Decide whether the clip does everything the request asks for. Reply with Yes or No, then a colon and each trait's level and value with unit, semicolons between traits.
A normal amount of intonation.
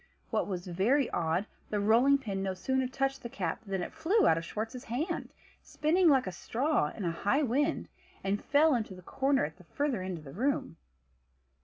No: wide, 7.0 semitones